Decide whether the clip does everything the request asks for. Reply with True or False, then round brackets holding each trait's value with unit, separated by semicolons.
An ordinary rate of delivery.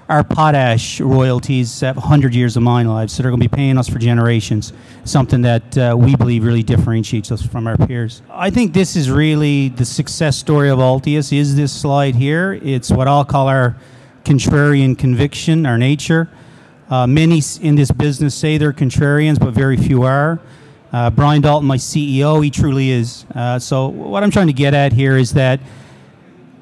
True (185 wpm)